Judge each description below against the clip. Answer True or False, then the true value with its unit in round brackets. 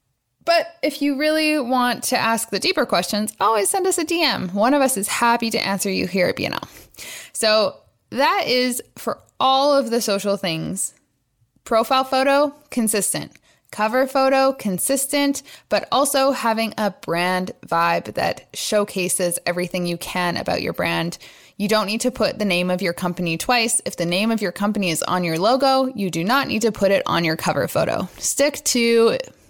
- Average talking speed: True (180 wpm)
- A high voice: True (225 Hz)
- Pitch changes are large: True (6.5 semitones)